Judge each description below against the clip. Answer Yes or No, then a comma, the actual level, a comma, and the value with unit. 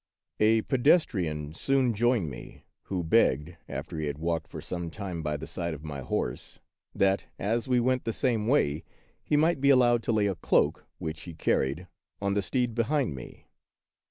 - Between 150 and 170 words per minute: No, average, 185 wpm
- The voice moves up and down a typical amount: No, wide, 7.4 semitones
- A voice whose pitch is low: Yes, low, 100 Hz